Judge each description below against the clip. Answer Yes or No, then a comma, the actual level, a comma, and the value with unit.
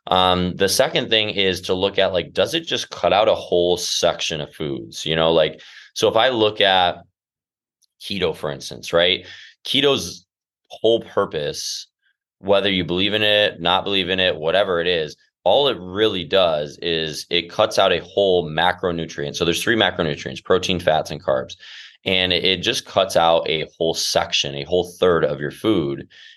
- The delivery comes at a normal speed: Yes, average, 180 wpm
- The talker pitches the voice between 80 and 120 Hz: Yes, very low, 90 Hz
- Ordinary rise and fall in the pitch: Yes, average, 3.0 semitones